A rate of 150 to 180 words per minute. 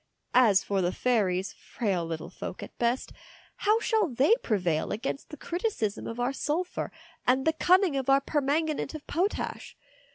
Yes: average, 160 wpm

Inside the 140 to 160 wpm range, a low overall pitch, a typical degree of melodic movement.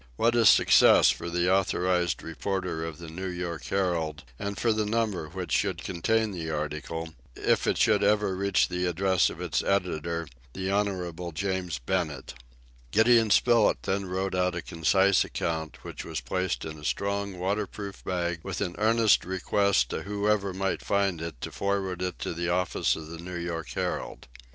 No: average, 175 wpm; very low, 90 Hz; average, 3.0 semitones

